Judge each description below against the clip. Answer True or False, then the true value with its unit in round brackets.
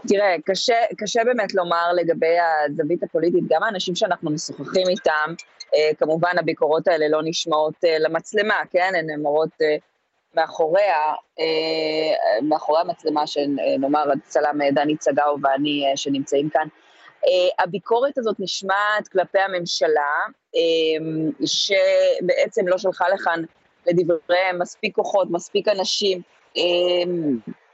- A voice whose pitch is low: False (170 Hz)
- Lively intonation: False (3.8 semitones)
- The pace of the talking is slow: True (95 wpm)